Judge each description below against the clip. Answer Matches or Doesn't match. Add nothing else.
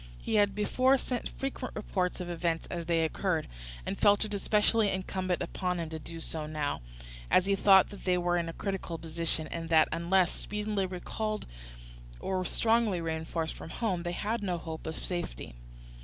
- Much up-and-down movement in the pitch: Doesn't match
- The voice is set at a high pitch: Doesn't match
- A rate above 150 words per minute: Matches